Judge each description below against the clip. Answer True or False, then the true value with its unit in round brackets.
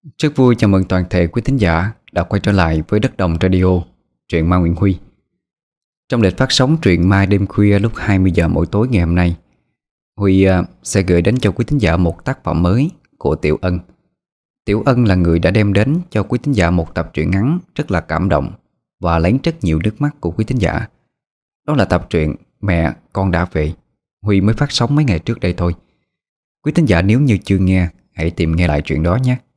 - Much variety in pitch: True (6.3 semitones)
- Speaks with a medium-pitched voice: False (95 Hz)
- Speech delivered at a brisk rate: False (225 wpm)